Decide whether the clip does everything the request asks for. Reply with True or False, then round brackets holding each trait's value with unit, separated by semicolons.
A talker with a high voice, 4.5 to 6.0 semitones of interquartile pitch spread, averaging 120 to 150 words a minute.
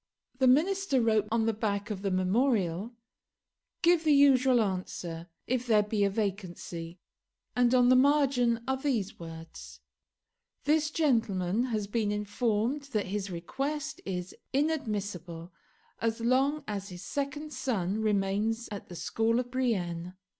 True (220 Hz; 5.1 semitones; 140 wpm)